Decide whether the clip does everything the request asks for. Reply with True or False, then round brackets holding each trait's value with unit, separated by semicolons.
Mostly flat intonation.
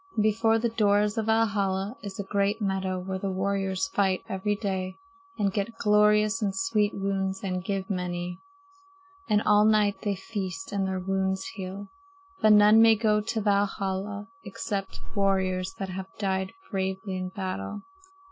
True (1.7 semitones)